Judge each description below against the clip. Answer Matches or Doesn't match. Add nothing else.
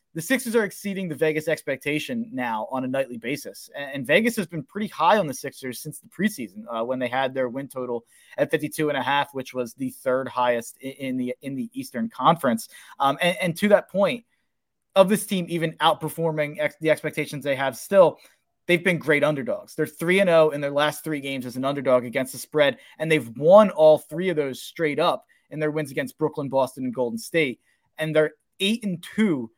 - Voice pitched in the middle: Matches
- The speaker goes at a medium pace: Doesn't match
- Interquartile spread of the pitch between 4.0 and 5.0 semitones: Matches